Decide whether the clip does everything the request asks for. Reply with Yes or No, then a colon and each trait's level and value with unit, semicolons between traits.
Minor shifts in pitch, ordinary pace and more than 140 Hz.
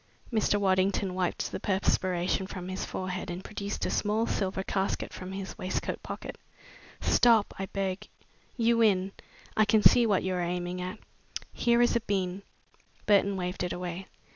Yes: narrow, 2.0 semitones; average, 165 wpm; high, 190 Hz